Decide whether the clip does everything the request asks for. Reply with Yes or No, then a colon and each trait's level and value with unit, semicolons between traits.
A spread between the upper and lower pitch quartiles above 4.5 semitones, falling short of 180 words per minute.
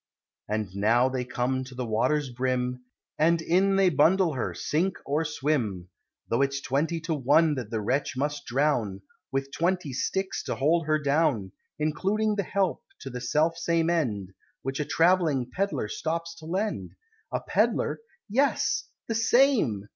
Yes: average, 5.1 semitones; average, 160 wpm